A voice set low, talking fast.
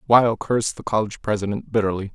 No: low, 105 Hz; average, 170 wpm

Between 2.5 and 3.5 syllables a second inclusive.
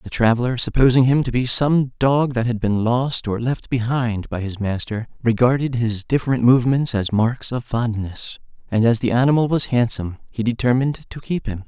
No: 5.2 syllables/s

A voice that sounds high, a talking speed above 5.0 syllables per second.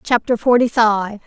No: high, 225 Hz; 4.4 syllables/s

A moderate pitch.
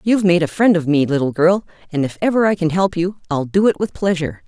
Yes: medium, 175 Hz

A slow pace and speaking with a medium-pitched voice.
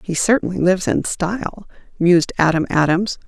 No: average, 145 wpm; medium, 180 Hz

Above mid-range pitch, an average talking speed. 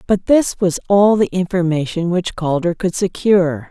No: medium, 180 Hz; average, 160 wpm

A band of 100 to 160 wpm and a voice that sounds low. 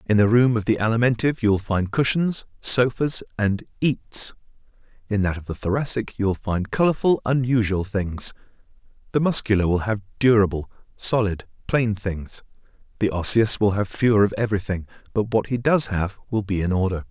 No: average, 170 wpm; low, 110 Hz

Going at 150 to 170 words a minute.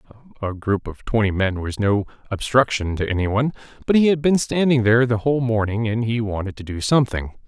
No: average, 200 wpm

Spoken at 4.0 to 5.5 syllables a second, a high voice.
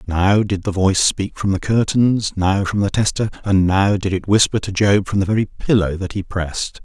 No: 5.1 syllables/s; low, 100 Hz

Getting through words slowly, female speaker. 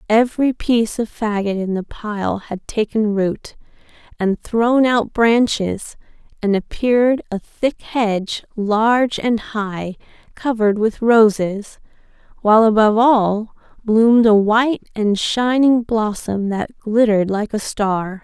Yes: slow, 130 wpm; female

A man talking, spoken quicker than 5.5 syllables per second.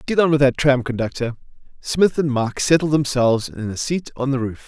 Yes: male; 5.9 syllables/s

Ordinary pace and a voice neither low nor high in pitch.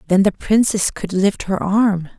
No: average, 190 wpm; high, 195 Hz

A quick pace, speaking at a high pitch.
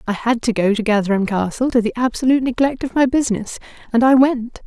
Yes: fast, 220 wpm; high, 235 Hz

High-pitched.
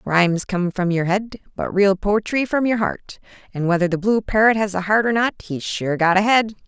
Yes: high, 200 Hz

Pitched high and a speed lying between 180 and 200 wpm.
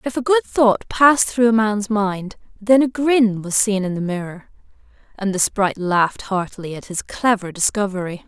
Yes: high, 210 Hz; average, 190 wpm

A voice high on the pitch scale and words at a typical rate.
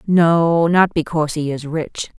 No: medium, 160 Hz; average, 165 wpm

